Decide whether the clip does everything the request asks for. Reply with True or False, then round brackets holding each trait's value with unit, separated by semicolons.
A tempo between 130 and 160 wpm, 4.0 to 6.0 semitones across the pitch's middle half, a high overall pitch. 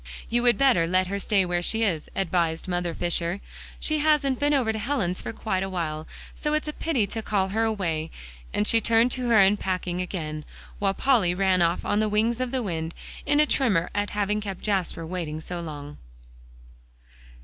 False (195 wpm; 4.6 semitones; 195 Hz)